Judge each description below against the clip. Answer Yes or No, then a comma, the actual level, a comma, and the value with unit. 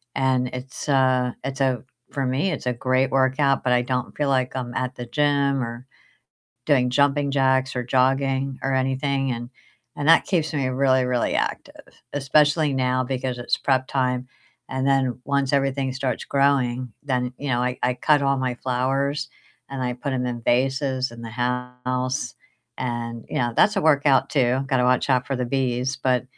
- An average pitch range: No, narrow, 1.6 semitones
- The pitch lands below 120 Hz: No, low, 130 Hz